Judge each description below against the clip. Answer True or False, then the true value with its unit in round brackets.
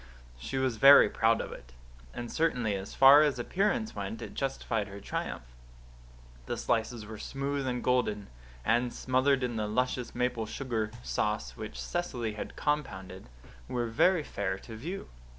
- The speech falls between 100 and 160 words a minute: True (155 wpm)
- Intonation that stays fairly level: False (4.2 semitones)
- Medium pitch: False (120 Hz)